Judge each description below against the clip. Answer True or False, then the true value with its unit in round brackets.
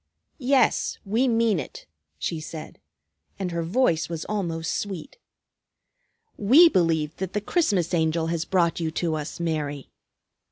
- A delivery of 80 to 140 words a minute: True (135 wpm)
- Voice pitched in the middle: True (170 Hz)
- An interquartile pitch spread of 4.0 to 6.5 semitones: True (4.4 semitones)